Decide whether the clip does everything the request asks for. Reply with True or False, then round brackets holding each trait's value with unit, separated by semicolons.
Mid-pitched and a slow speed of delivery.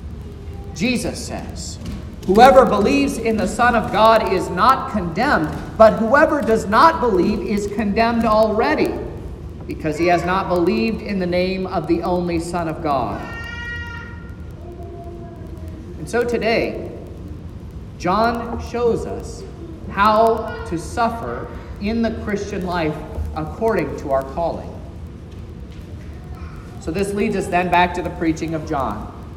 True (175 Hz; 125 wpm)